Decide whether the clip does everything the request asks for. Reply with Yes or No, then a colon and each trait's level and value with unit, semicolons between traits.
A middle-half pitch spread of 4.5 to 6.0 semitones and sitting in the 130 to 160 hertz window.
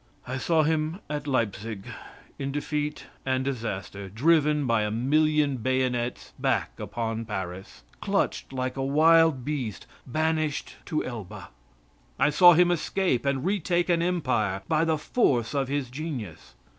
Yes: average, 4.8 semitones; medium, 140 Hz